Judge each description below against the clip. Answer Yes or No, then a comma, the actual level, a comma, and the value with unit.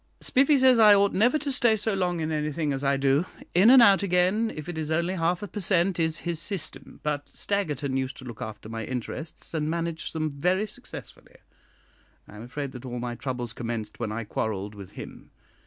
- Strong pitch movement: Yes, wide, 6.8 semitones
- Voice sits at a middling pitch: Yes, medium, 160 Hz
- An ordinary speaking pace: No, fast, 210 wpm